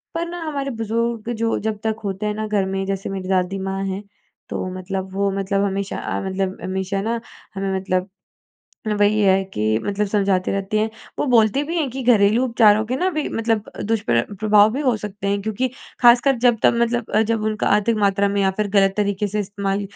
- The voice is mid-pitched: No, high, 205 Hz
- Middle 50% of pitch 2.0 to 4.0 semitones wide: Yes, average, 2.7 semitones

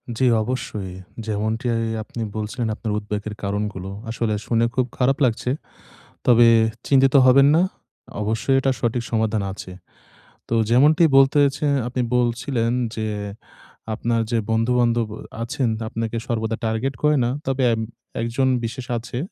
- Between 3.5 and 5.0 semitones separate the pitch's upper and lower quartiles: No, average, 2.7 semitones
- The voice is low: Yes, low, 115 Hz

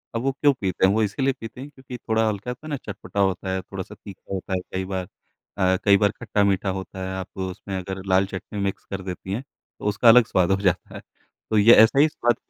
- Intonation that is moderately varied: Yes, average, 3.1 semitones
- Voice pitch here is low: Yes, low, 100 Hz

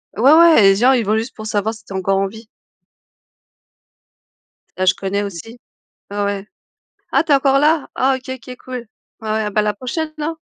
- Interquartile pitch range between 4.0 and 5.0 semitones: Yes, average, 4.7 semitones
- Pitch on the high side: Yes, high, 220 Hz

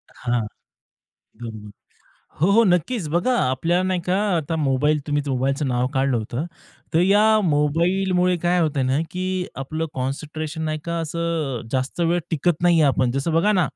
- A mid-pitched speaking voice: Yes, medium, 160 Hz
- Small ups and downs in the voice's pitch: No, average, 4.5 semitones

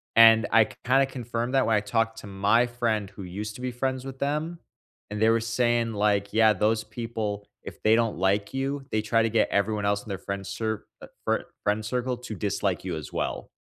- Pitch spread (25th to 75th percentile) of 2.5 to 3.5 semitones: Yes, average, 2.9 semitones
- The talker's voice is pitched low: Yes, low, 110 Hz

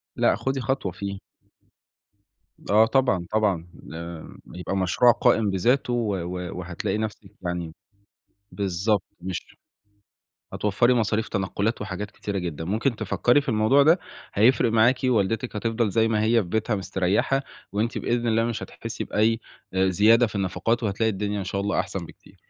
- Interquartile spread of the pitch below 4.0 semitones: Yes, average, 3.3 semitones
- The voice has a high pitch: No, low, 105 Hz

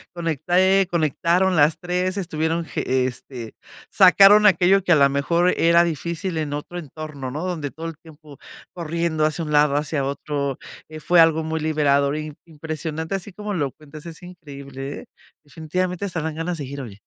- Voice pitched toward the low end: No, medium, 160 Hz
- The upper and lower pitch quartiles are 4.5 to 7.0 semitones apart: No, average, 3.2 semitones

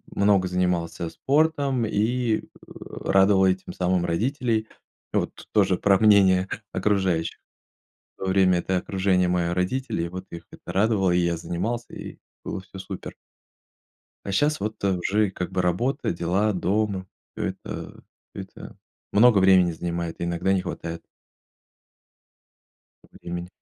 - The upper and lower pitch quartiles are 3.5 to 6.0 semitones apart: No, average, 3.1 semitones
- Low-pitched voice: Yes, very low, 95 Hz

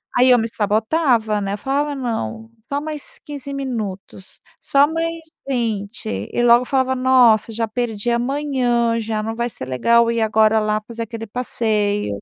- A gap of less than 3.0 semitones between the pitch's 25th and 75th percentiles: No, average, 3.3 semitones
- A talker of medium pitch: No, high, 230 Hz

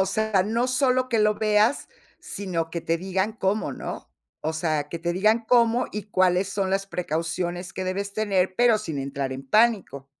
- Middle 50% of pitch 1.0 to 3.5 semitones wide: No, average, 4.1 semitones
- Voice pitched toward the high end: Yes, high, 195 Hz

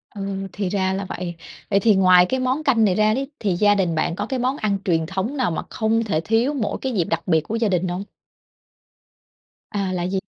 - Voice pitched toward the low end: No, high, 200 Hz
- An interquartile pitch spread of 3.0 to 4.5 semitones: Yes, average, 3.9 semitones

